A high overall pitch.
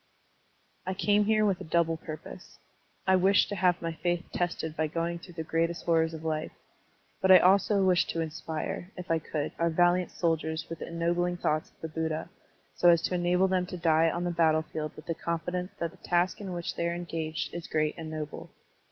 No: medium, 170 Hz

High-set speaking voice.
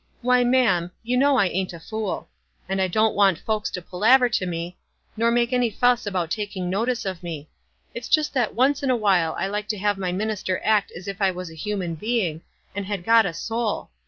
Yes: high, 205 Hz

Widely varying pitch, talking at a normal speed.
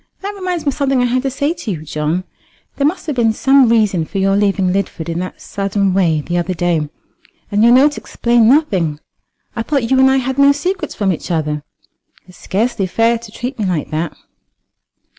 No: wide, 6.8 semitones; fast, 210 wpm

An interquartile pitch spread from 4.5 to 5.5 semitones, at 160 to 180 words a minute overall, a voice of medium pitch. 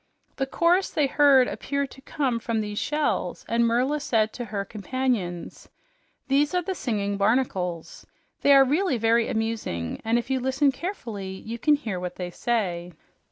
No: average, 5.1 semitones; average, 165 wpm; high, 235 Hz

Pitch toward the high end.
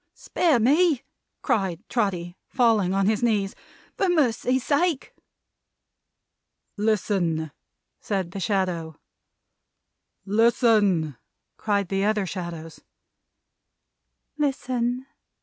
Yes: high, 210 Hz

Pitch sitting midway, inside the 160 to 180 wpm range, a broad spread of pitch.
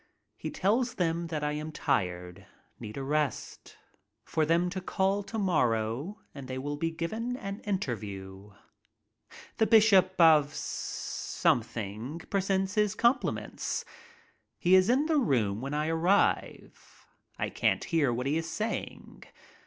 No: medium, 165 Hz; slow, 135 wpm; wide, 7.2 semitones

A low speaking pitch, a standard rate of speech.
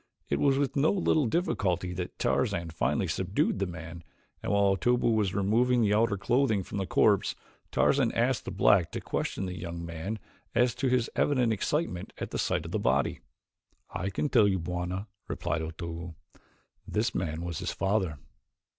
Yes: low, 100 Hz; average, 175 wpm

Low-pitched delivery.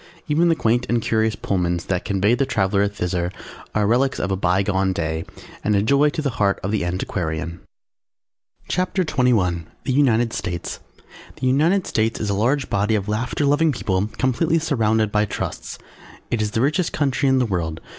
Yes: low, 110 Hz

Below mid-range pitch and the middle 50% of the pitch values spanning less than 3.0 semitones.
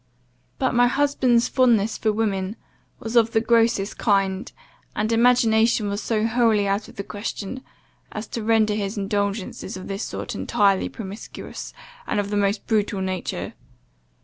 No: high, 215 Hz; narrow, 2.4 semitones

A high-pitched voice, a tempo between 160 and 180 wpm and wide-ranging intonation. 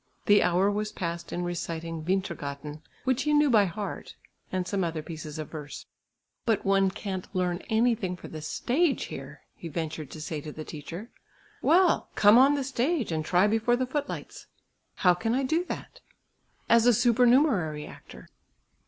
Yes: high, 195 Hz; average, 170 wpm; wide, 6.6 semitones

